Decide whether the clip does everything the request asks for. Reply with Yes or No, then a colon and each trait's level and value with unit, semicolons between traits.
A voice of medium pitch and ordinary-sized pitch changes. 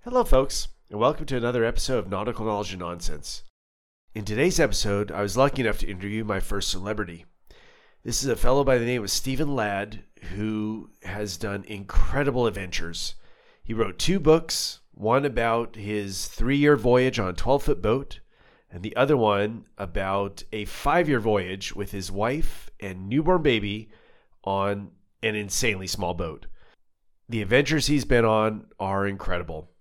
No: low, 105 Hz; average, 3.7 semitones